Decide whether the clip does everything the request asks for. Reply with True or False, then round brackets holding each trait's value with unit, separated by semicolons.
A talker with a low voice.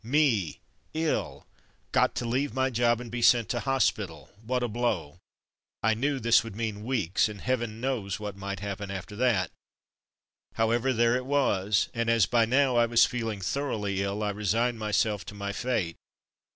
True (115 Hz)